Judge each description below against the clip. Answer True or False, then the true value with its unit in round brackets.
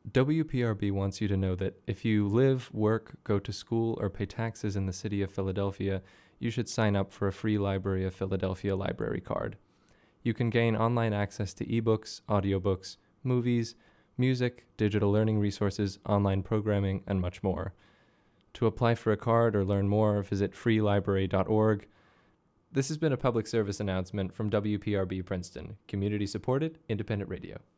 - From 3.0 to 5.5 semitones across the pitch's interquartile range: False (2.6 semitones)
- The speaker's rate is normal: True (160 wpm)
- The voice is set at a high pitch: False (105 Hz)